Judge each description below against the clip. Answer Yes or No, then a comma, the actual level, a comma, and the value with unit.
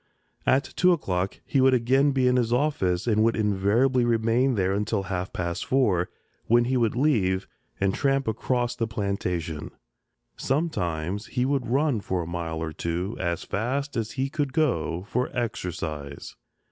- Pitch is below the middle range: Yes, low, 110 Hz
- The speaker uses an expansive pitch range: Yes, wide, 6.1 semitones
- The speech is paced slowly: No, average, 160 wpm